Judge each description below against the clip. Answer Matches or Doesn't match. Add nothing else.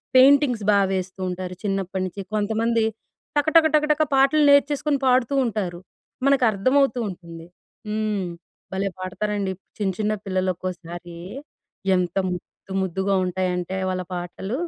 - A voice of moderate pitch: Doesn't match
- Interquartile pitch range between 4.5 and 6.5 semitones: Matches